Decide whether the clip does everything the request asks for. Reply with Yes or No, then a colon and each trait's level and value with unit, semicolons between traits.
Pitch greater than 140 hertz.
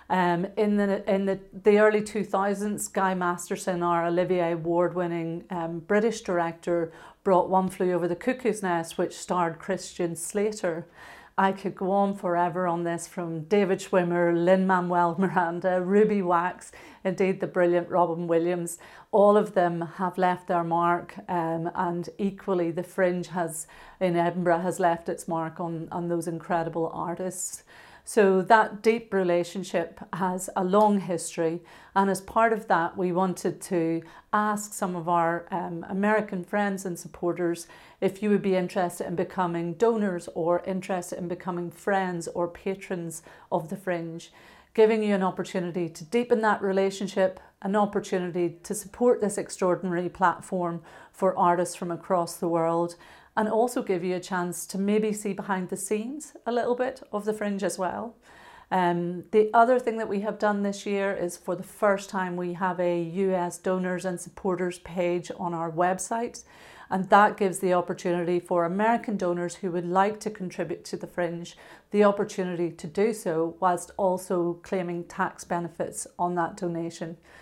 Yes: medium, 185 Hz